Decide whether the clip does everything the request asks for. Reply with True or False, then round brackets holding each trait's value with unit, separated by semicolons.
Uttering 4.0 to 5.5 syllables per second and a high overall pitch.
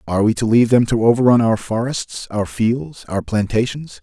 False (5.2 syllables/s; 115 Hz)